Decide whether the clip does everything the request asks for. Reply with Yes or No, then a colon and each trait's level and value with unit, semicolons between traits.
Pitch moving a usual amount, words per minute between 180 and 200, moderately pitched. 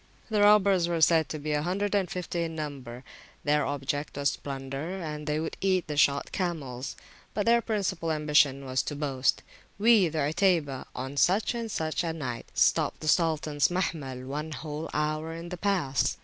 Yes: average, 4.0 semitones; average, 185 wpm; medium, 155 Hz